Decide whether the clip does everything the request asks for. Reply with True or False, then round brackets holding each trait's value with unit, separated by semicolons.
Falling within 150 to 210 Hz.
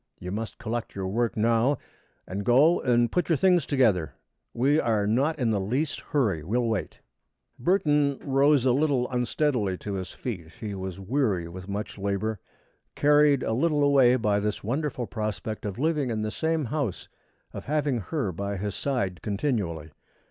False (120 Hz)